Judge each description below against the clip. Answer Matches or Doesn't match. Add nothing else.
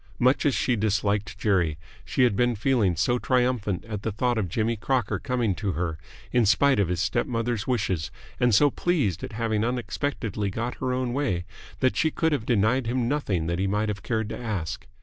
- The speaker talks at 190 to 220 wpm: Matches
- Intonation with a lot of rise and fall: Doesn't match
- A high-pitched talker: Doesn't match